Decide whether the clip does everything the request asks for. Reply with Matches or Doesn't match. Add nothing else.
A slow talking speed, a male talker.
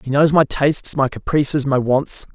Doesn't match